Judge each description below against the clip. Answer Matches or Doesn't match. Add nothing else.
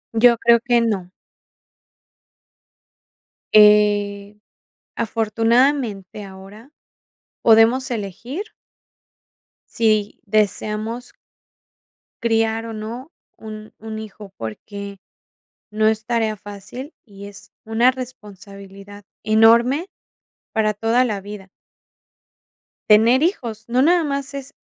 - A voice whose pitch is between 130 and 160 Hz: Doesn't match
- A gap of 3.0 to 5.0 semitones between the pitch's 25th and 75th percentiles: Doesn't match